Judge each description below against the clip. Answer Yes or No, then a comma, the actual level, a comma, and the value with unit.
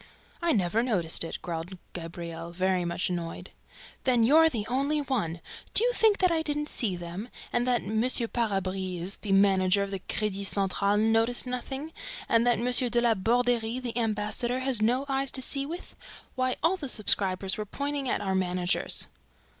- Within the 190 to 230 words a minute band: No, average, 175 wpm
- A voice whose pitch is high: Yes, high, 225 Hz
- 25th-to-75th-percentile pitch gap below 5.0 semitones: No, average, 5.3 semitones